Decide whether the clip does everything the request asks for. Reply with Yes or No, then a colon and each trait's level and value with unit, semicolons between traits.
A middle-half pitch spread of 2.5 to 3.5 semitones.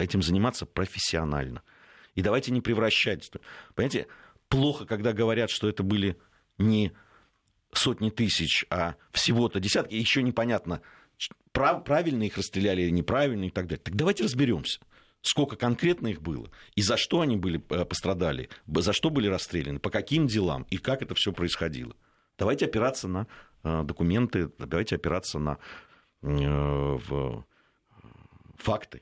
No: average, 5.2 semitones